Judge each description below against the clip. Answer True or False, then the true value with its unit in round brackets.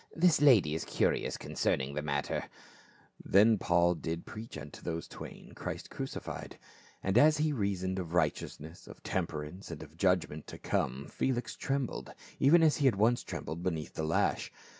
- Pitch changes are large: True (7.6 semitones)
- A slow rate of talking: False (170 wpm)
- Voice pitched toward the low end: True (90 Hz)